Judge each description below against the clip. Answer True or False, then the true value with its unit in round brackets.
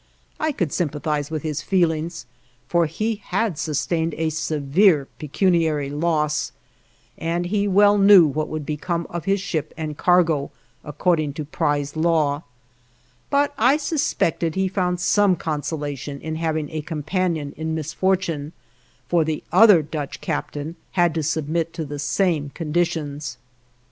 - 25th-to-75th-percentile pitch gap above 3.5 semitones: False (3.1 semitones)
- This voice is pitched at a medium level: True (160 Hz)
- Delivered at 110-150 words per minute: True (140 wpm)